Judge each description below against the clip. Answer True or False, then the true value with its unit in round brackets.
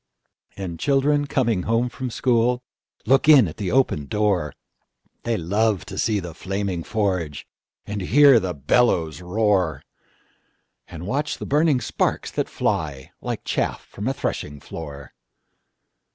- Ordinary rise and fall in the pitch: False (6.4 semitones)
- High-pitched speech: False (105 Hz)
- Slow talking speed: True (120 wpm)